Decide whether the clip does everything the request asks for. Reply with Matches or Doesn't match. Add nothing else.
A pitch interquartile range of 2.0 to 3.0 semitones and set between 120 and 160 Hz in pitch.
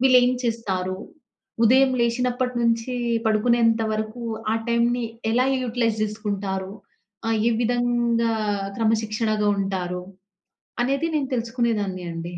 Doesn't match